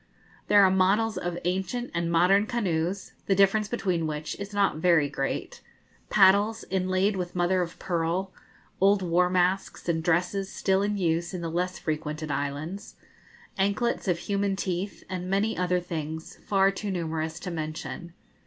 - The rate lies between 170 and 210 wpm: No, average, 155 wpm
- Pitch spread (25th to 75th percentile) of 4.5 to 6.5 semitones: No, average, 2.8 semitones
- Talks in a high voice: No, medium, 180 Hz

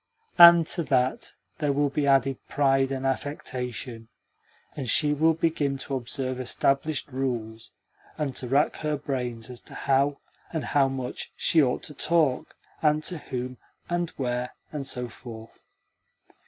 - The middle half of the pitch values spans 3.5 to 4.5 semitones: No, average, 2.8 semitones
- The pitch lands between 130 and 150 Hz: Yes, low, 135 Hz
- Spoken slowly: No, average, 150 wpm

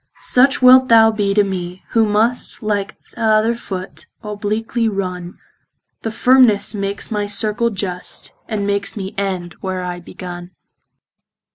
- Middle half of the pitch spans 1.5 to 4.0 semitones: Yes, average, 2.9 semitones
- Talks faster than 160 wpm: No, average, 140 wpm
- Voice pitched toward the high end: Yes, high, 205 Hz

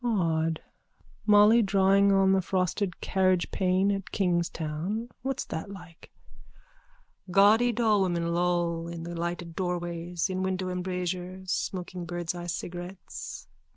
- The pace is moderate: No, slow, 115 wpm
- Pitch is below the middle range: No, medium, 180 Hz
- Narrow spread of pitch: Yes, narrow, 2.1 semitones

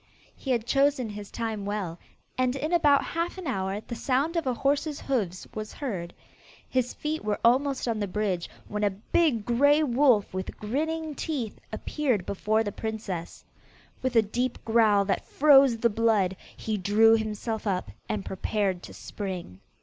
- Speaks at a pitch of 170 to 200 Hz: No, high, 225 Hz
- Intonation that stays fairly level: No, average, 5.0 semitones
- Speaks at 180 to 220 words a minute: No, average, 165 wpm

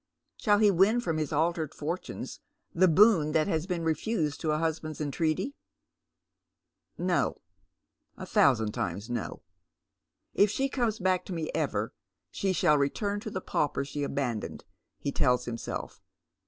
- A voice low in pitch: No, medium, 160 Hz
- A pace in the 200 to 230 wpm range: No, average, 150 wpm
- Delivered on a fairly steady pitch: No, average, 4.6 semitones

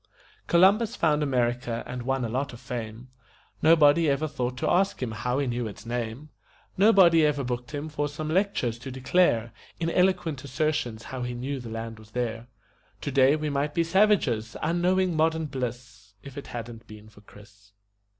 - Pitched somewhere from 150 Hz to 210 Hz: No, low, 130 Hz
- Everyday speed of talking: Yes, average, 175 wpm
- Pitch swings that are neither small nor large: Yes, average, 4.8 semitones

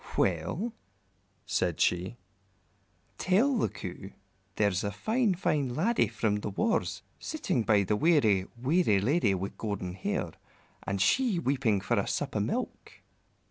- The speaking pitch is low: Yes, low, 110 Hz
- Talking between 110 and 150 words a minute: Yes, average, 140 wpm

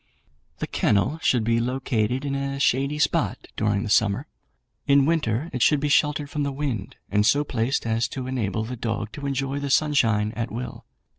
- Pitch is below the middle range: Yes, low, 130 Hz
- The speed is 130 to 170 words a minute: No, average, 190 wpm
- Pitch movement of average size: Yes, average, 4.1 semitones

